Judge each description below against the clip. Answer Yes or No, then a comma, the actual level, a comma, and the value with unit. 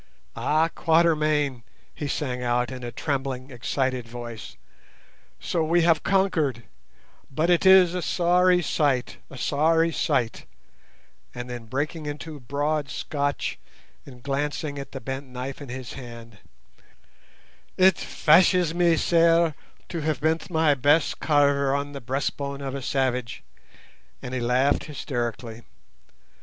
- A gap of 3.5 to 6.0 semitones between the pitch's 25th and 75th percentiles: Yes, average, 4.1 semitones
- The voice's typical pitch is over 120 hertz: Yes, medium, 140 Hz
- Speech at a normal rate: No, slow, 130 wpm